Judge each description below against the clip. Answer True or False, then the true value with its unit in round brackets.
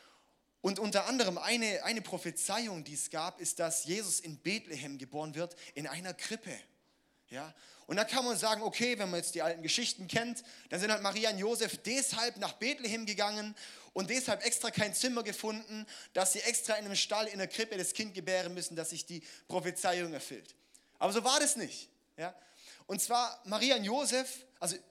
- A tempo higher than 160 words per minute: True (190 wpm)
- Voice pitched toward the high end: True (205 Hz)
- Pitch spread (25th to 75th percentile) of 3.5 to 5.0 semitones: True (4.3 semitones)